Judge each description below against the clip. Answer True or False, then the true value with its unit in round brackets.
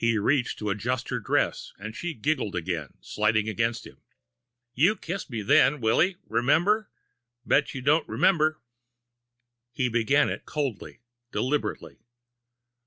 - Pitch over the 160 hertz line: False (125 Hz)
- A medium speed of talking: False (130 wpm)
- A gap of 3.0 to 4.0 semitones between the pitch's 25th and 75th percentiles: False (5.6 semitones)